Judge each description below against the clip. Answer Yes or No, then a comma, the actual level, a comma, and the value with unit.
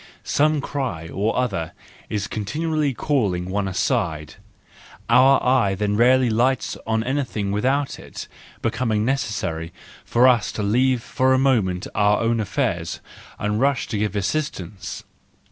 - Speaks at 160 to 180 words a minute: No, slow, 135 wpm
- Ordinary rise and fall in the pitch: Yes, average, 4.7 semitones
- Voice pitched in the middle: No, low, 115 Hz